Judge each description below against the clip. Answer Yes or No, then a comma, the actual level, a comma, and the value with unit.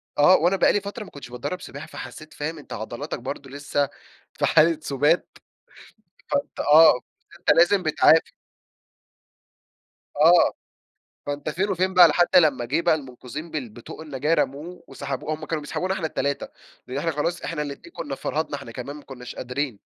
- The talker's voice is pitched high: No, medium, 150 Hz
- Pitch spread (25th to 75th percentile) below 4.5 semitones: Yes, average, 3.5 semitones